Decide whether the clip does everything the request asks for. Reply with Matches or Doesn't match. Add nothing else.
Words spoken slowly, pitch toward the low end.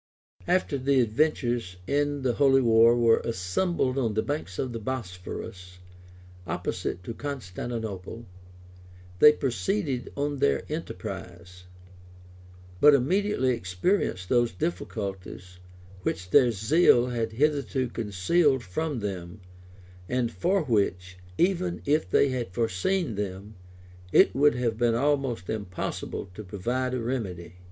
Matches